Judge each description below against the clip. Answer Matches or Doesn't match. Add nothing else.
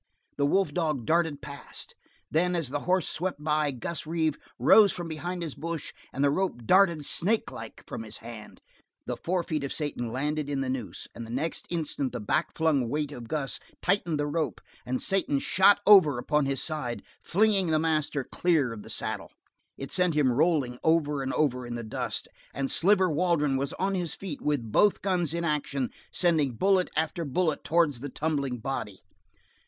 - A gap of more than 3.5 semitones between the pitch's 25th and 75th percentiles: Matches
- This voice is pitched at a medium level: Matches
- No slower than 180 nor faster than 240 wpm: Matches